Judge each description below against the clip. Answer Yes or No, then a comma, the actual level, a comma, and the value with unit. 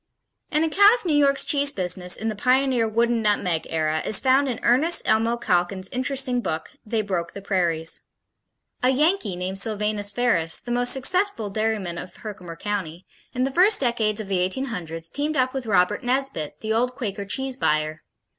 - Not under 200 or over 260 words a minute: No, average, 175 wpm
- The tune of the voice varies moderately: No, wide, 6.1 semitones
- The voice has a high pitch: Yes, high, 220 Hz